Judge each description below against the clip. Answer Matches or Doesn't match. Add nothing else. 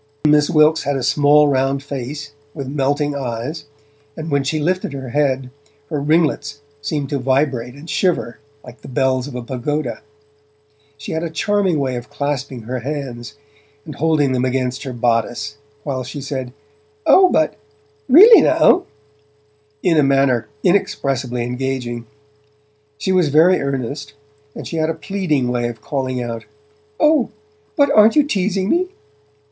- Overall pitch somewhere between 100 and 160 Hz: Matches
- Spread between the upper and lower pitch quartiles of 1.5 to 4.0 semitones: Matches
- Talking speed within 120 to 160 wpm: Matches